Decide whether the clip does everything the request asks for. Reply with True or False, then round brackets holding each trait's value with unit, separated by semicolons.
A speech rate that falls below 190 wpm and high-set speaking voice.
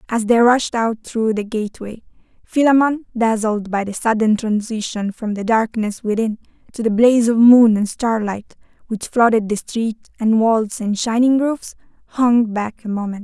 True (170 wpm; 225 Hz)